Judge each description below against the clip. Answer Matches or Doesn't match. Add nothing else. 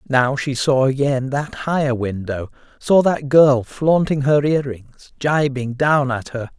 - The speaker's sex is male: Matches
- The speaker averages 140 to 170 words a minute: Matches